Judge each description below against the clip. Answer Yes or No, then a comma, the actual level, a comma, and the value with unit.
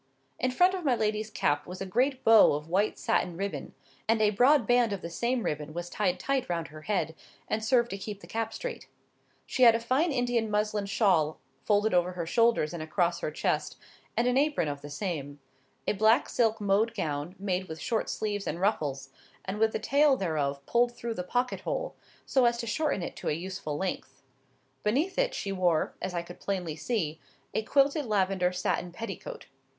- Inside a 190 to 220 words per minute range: Yes, average, 200 wpm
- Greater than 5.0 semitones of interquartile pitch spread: Yes, wide, 5.4 semitones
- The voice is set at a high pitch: Yes, high, 205 Hz